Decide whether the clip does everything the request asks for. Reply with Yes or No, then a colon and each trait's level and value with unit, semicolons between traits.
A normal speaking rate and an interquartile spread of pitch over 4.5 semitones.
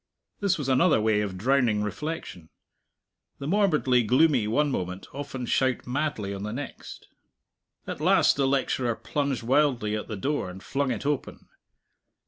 Yes: average, 150 wpm; average, 5.3 semitones